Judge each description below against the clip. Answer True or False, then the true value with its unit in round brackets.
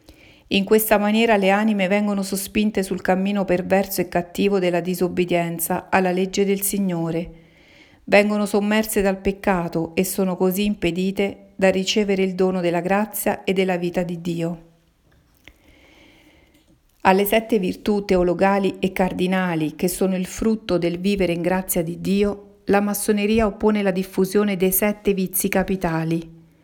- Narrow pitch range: True (2.1 semitones)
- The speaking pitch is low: False (190 Hz)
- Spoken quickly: False (140 wpm)